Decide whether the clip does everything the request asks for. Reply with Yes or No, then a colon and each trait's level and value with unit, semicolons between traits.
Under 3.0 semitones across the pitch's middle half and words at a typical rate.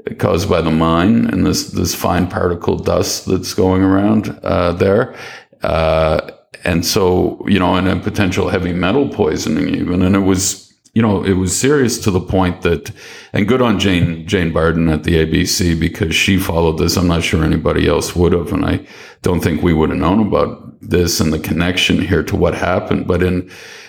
Yes: narrow, 2.4 semitones; average, 195 wpm